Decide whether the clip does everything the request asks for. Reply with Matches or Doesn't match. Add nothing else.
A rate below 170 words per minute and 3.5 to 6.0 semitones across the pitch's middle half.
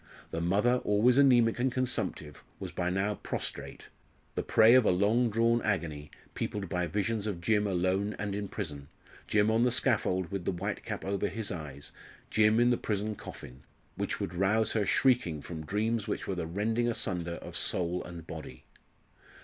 Doesn't match